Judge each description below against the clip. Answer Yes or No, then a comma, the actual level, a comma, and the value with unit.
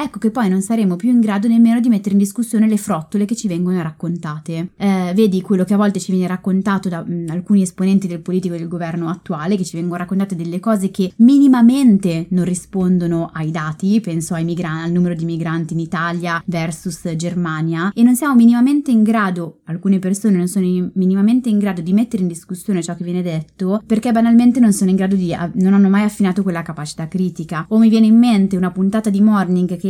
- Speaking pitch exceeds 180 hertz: Yes, high, 190 Hz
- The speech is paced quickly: Yes, fast, 215 wpm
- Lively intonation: No, average, 3.4 semitones